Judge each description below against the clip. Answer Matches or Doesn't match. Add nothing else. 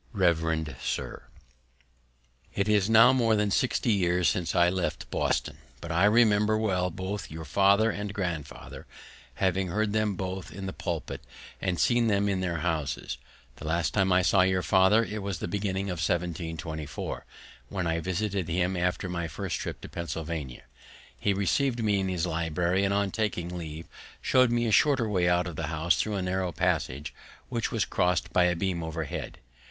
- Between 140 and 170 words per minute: Doesn't match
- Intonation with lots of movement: Doesn't match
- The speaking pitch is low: Matches